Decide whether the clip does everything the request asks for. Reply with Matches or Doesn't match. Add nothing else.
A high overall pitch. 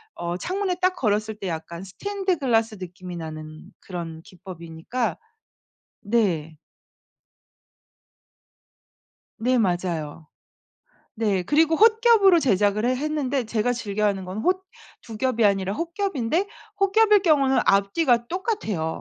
Matches